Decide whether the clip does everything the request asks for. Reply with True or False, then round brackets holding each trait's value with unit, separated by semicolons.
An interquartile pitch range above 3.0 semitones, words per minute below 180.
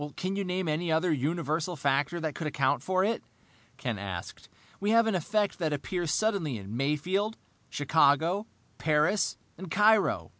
True (5.0 semitones; 155 wpm)